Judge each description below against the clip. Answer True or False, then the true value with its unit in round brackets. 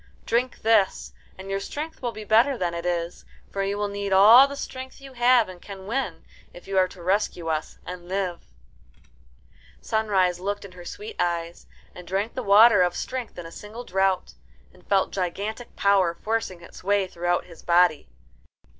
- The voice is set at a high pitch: True (195 Hz)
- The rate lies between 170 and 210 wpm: True (180 wpm)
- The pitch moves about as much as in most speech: True (3.9 semitones)